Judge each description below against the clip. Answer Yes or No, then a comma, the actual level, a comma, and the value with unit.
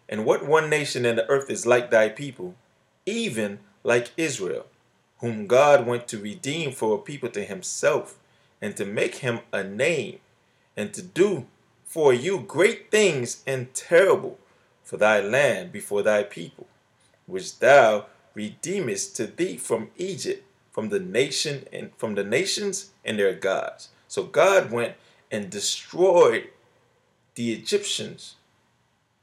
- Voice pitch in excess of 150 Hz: No, low, 135 Hz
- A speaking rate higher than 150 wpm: No, average, 140 wpm